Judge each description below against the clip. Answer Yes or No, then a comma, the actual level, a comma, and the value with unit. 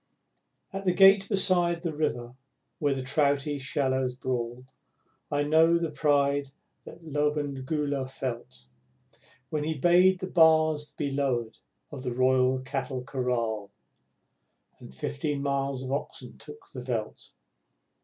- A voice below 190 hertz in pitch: Yes, medium, 140 Hz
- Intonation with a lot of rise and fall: No, average, 3.4 semitones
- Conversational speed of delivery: No, slow, 125 wpm